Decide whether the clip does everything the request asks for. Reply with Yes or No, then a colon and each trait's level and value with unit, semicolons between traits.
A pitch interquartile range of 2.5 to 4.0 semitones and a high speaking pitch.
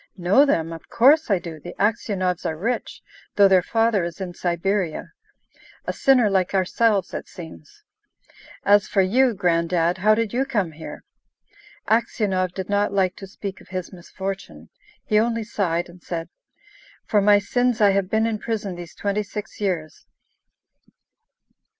Yes: average, 3.4 semitones; high, 195 Hz